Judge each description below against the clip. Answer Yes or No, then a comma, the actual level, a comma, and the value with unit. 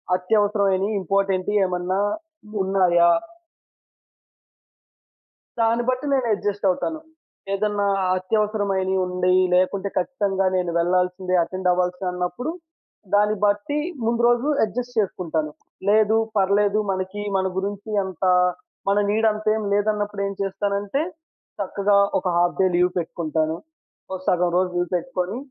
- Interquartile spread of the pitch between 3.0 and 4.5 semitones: No, narrow, 2.4 semitones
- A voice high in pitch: Yes, high, 195 Hz